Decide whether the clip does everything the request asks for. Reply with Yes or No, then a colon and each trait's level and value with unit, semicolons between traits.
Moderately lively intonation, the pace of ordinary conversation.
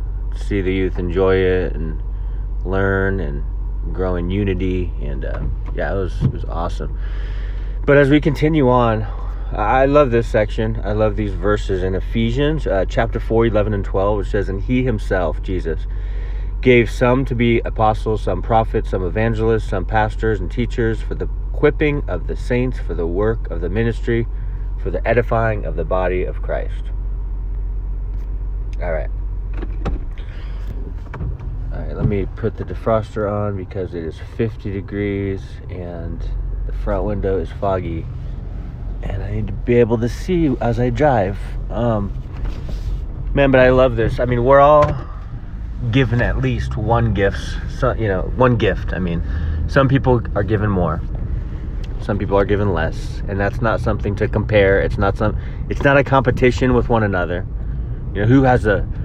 Yes: average, 3.5 semitones; average, 165 wpm